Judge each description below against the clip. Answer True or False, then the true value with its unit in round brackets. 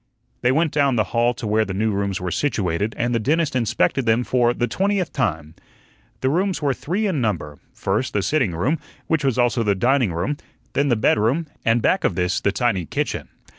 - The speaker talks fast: True (210 wpm)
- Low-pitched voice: True (120 Hz)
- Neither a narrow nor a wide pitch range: False (5.7 semitones)